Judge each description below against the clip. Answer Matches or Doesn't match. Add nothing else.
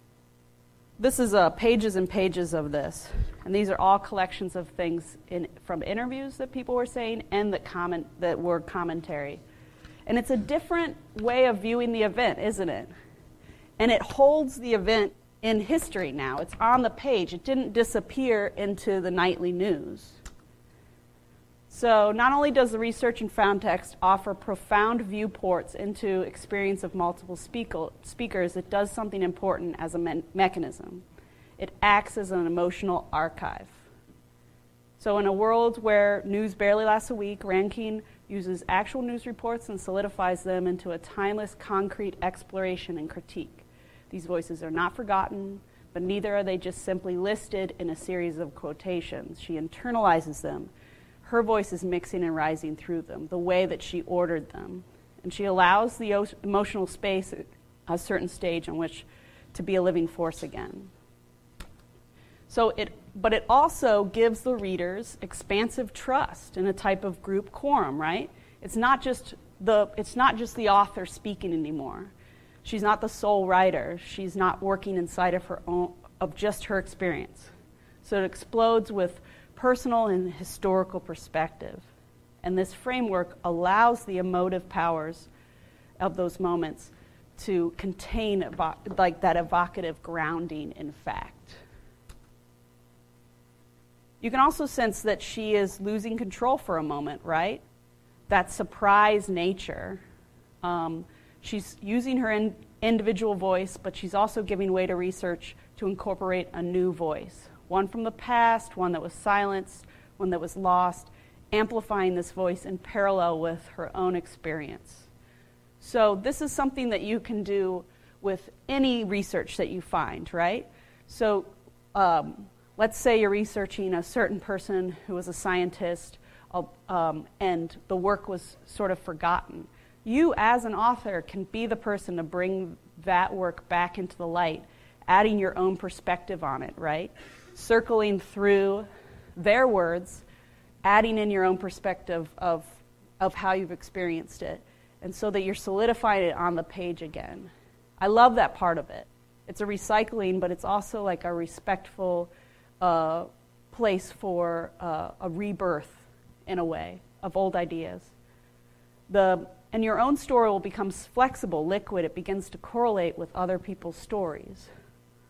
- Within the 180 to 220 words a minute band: Doesn't match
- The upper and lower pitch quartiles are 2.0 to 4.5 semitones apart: Matches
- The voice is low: Doesn't match